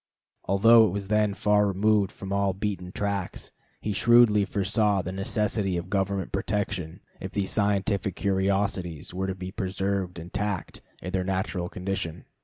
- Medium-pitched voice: No, very low, 95 Hz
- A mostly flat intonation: Yes, narrow, 1.7 semitones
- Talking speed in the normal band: Yes, average, 150 wpm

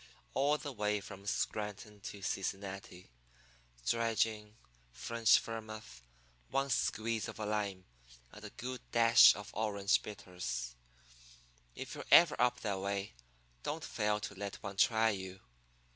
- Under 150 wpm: Yes, slow, 135 wpm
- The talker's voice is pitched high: No, low, 105 Hz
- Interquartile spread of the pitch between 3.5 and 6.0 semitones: No, narrow, 2.6 semitones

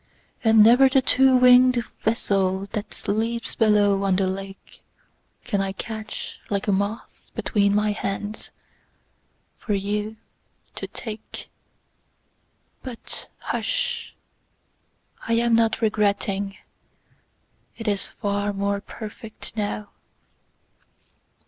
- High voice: Yes, high, 210 Hz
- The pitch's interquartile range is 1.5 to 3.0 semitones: Yes, narrow, 2.4 semitones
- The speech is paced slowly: Yes, slow, 90 wpm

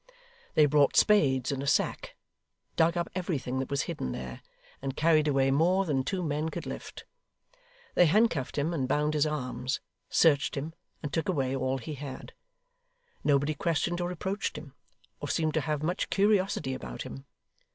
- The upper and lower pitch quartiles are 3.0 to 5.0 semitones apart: Yes, average, 3.9 semitones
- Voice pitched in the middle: Yes, medium, 150 Hz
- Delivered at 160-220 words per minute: Yes, average, 170 wpm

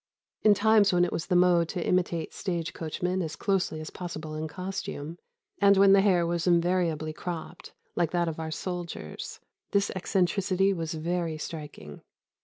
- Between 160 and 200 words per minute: Yes, average, 165 wpm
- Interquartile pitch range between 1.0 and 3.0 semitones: Yes, narrow, 2.6 semitones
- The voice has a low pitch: No, medium, 175 Hz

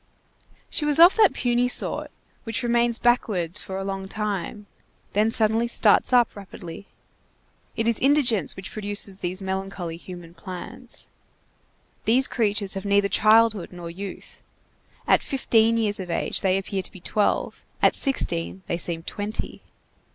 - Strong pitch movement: No, average, 3.7 semitones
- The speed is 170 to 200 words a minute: No, average, 145 wpm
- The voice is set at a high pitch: Yes, high, 205 Hz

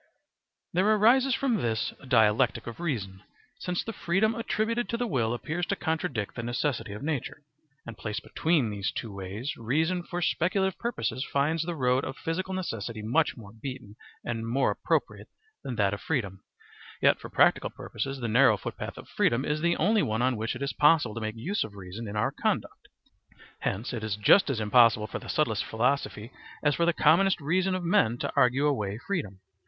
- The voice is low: Yes, low, 130 Hz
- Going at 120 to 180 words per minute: No, average, 190 wpm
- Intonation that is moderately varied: No, wide, 7.6 semitones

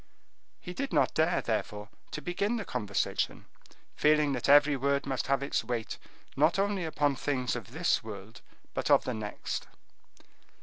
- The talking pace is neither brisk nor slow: Yes, average, 160 wpm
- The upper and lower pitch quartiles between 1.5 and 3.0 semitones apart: No, average, 4.2 semitones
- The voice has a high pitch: No, medium, 140 Hz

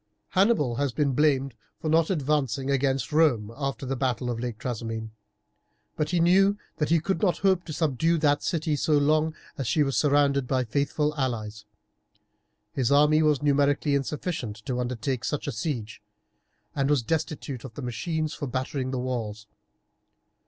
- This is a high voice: No, medium, 140 Hz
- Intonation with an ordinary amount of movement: Yes, average, 3.5 semitones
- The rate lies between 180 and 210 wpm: No, average, 165 wpm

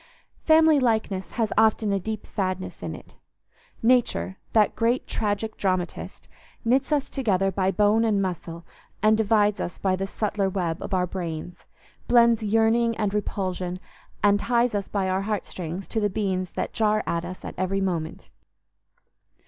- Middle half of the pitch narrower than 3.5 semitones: Yes, average, 3.0 semitones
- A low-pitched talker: No, high, 205 Hz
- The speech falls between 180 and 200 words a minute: No, average, 155 wpm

